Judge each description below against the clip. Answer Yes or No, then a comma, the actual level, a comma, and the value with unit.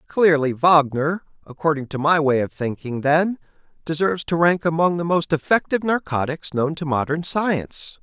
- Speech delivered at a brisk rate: No, average, 155 wpm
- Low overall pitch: No, medium, 160 Hz